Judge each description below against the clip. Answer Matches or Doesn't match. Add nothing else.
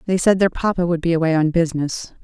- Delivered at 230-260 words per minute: Matches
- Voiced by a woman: Matches